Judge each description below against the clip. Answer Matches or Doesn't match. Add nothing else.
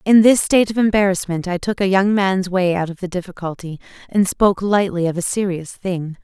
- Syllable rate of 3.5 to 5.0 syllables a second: Doesn't match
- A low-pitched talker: Doesn't match